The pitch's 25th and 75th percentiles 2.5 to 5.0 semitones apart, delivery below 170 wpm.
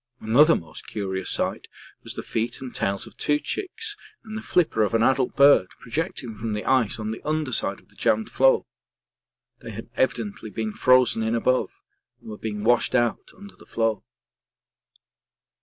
No: average, 3.7 semitones; average, 175 wpm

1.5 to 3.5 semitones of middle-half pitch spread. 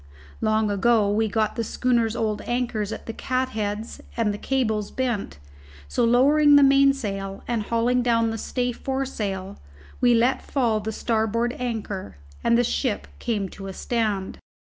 Yes: average, 2.9 semitones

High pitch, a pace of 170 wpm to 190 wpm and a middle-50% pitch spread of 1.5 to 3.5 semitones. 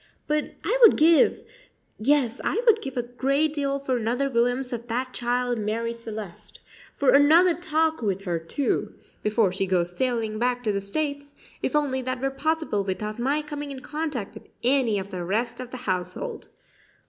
No: very high, 250 Hz; average, 180 wpm; average, 4.9 semitones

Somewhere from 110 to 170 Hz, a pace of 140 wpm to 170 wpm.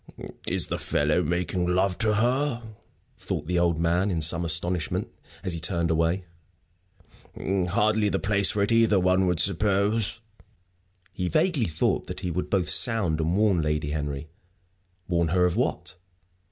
No: very low, 90 Hz; average, 155 wpm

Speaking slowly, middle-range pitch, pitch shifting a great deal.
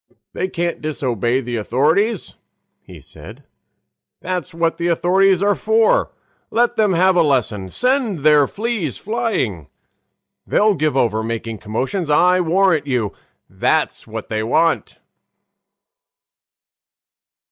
Yes: slow, 115 wpm; medium, 165 Hz; wide, 7.7 semitones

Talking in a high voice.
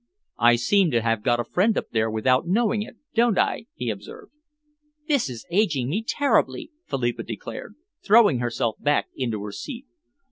No: medium, 140 Hz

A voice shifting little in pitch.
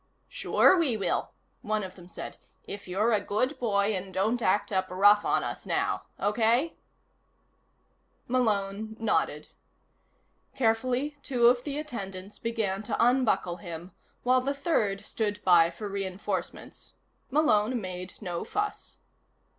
No: average, 4.2 semitones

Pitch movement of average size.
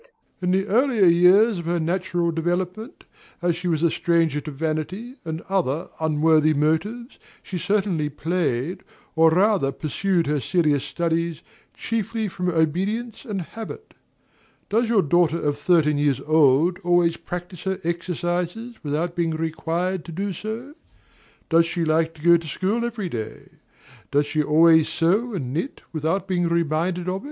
Yes: average, 3.2 semitones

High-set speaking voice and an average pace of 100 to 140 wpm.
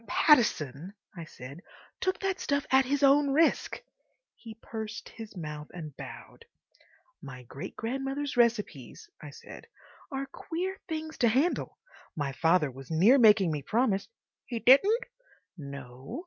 Yes: high, 225 Hz; slow, 135 wpm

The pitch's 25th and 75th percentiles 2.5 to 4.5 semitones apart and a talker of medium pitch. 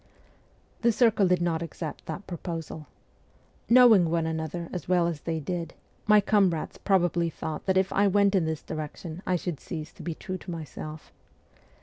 Yes: average, 3.0 semitones; medium, 175 Hz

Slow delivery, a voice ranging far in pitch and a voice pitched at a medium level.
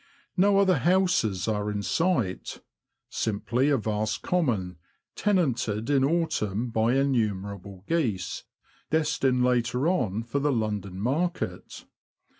No: slow, 115 wpm; wide, 6.9 semitones; low, 120 Hz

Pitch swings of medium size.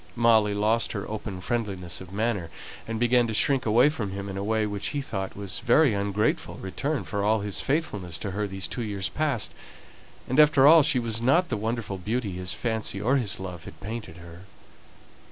Yes: average, 3.6 semitones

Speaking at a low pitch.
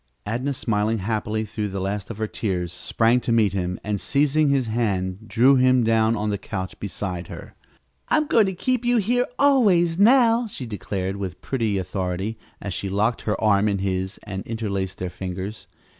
Yes: low, 110 Hz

